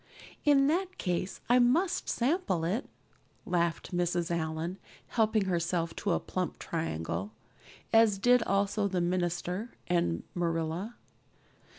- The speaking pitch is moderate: Yes, medium, 180 Hz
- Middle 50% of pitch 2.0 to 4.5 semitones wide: No, average, 4.9 semitones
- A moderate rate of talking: No, slow, 115 wpm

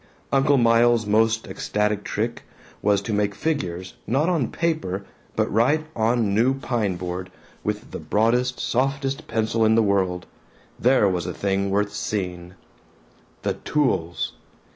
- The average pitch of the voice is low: Yes, low, 110 Hz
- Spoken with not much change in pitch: No, average, 4.2 semitones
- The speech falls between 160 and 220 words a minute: No, average, 140 wpm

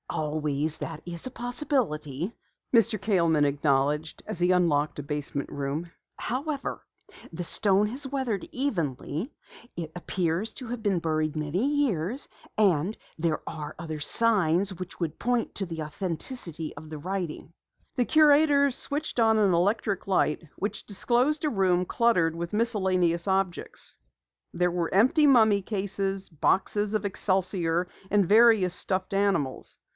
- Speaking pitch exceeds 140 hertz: Yes, medium, 185 Hz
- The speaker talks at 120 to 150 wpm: Yes, average, 140 wpm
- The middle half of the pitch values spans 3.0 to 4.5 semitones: No, wide, 5.5 semitones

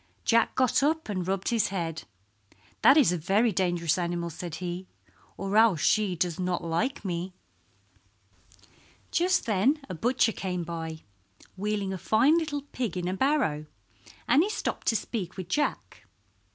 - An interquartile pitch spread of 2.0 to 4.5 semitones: No, wide, 5.6 semitones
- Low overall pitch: No, high, 190 Hz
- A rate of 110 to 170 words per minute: Yes, average, 155 wpm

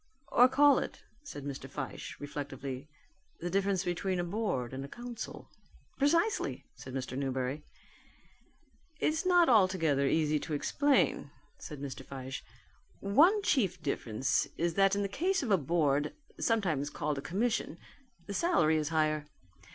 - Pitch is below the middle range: No, medium, 170 Hz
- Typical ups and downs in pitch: No, wide, 8.5 semitones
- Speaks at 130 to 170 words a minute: Yes, average, 145 wpm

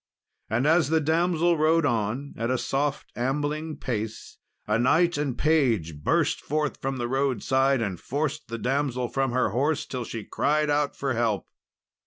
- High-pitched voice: No, low, 135 Hz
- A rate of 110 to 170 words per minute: Yes, average, 165 wpm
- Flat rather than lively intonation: No, average, 4.1 semitones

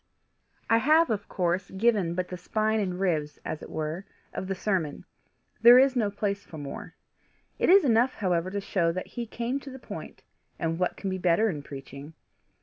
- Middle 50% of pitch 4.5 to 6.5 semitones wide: Yes, average, 5.1 semitones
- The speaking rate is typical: Yes, average, 195 wpm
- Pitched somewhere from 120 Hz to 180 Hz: No, high, 190 Hz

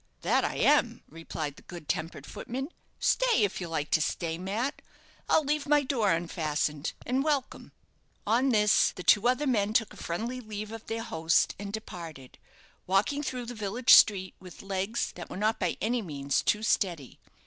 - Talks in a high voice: Yes, high, 205 Hz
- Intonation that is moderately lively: No, wide, 6.1 semitones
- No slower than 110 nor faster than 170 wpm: No, average, 180 wpm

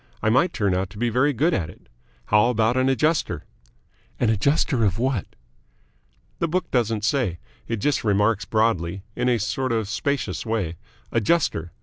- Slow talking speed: No, average, 165 wpm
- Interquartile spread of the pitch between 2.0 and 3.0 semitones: No, average, 4.2 semitones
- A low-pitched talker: Yes, low, 115 Hz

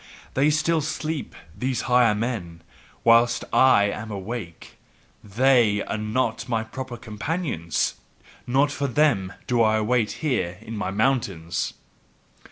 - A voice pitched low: Yes, low, 115 Hz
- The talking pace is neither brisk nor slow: No, slow, 125 wpm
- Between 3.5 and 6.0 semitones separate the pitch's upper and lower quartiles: Yes, average, 3.9 semitones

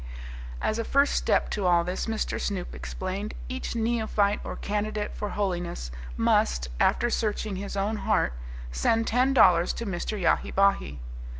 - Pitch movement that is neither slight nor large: Yes, average, 3.5 semitones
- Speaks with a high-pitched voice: Yes, high, 205 Hz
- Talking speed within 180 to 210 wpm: No, average, 155 wpm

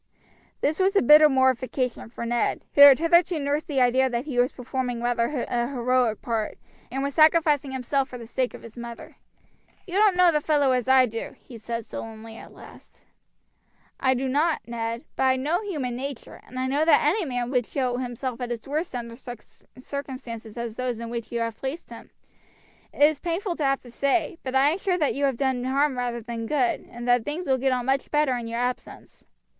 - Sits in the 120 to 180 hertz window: No, very high, 260 Hz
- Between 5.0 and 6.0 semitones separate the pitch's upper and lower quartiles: No, average, 3.4 semitones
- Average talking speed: No, fast, 215 wpm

